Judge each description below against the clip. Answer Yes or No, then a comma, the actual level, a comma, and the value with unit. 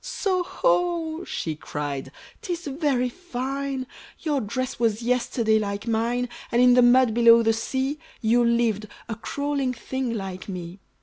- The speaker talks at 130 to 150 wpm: Yes, average, 145 wpm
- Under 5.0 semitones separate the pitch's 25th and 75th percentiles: Yes, average, 3.9 semitones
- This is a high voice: Yes, high, 245 Hz